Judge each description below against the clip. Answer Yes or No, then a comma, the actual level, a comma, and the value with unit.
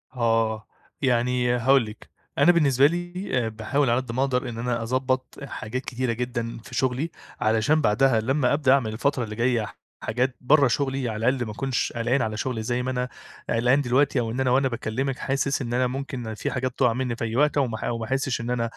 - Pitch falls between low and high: No, low, 125 Hz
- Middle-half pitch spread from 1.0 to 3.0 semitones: Yes, narrow, 2.5 semitones